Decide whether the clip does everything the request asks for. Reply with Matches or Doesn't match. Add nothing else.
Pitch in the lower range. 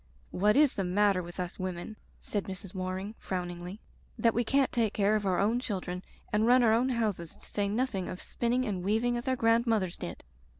Doesn't match